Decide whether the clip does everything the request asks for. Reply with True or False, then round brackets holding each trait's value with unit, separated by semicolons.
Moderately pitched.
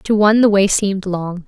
False (195 Hz)